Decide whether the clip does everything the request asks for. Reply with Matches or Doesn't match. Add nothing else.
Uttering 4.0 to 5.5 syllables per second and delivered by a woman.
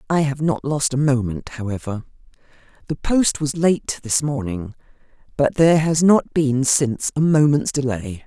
Matches